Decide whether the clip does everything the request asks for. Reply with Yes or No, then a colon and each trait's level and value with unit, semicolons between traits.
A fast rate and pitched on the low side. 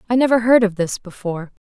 No: fast, 220 wpm; high, 215 Hz